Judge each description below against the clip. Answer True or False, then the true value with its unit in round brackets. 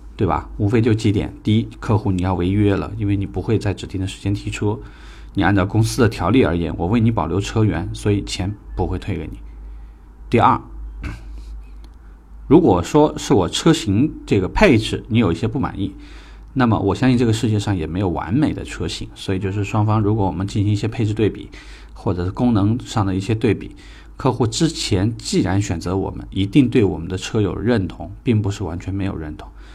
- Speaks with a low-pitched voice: True (100 Hz)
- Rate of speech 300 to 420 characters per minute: True (305 characters per minute)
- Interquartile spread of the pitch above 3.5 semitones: False (3.2 semitones)